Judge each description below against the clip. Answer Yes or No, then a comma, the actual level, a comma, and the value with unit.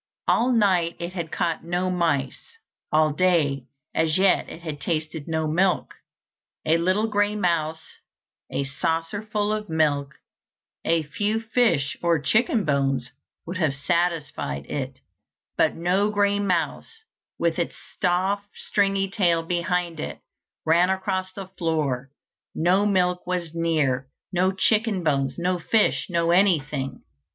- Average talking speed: No, slow, 130 wpm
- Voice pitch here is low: No, medium, 170 Hz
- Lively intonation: No, average, 3.8 semitones